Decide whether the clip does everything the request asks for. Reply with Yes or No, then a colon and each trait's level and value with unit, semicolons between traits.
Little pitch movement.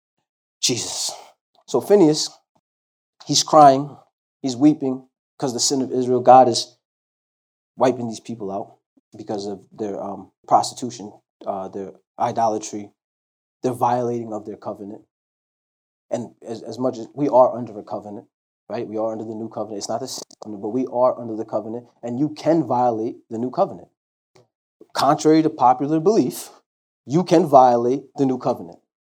No: average, 3.5 semitones